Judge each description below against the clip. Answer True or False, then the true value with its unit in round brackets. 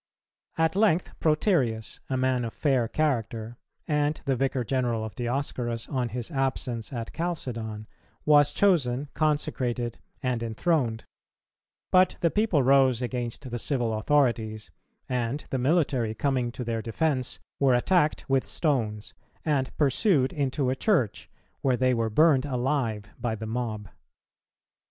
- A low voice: True (130 Hz)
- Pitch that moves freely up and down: False (3.9 semitones)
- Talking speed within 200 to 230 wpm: False (135 wpm)